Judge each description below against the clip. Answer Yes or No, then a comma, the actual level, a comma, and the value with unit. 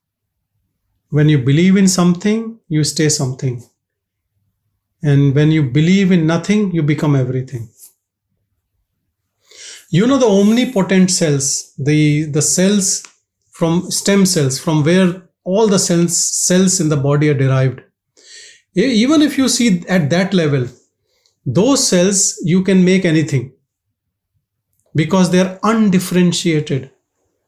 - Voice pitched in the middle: Yes, medium, 160 Hz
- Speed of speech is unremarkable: No, slow, 120 wpm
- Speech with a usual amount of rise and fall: No, wide, 6.5 semitones